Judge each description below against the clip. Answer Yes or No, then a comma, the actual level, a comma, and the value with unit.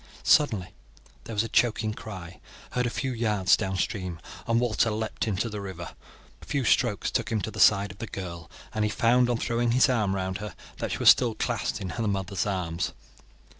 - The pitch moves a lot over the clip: No, average, 3.5 semitones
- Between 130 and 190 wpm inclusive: No, fast, 205 wpm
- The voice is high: No, low, 105 Hz